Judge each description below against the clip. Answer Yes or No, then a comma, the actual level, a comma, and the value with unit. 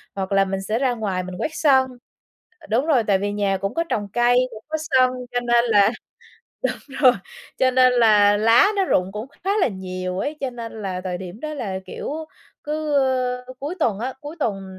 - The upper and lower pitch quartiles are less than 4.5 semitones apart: No, average, 5.1 semitones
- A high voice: Yes, high, 235 Hz